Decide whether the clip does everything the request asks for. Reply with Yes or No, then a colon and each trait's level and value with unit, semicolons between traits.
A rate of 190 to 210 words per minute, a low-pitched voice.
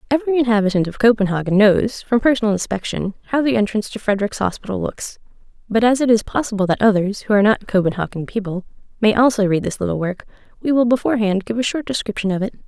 No: average, 200 wpm; high, 215 Hz